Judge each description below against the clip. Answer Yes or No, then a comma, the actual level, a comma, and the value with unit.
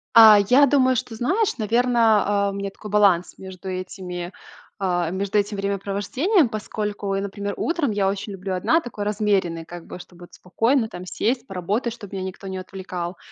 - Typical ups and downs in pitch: Yes, average, 3.1 semitones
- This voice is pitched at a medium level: No, high, 200 Hz